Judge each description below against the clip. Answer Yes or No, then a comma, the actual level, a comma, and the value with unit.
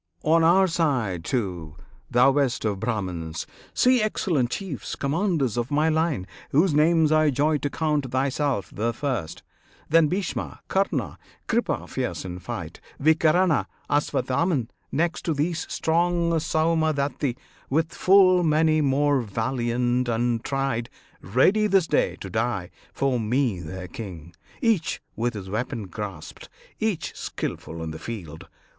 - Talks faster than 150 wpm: No, slow, 135 wpm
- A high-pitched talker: No, medium, 140 Hz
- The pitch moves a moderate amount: No, wide, 6.0 semitones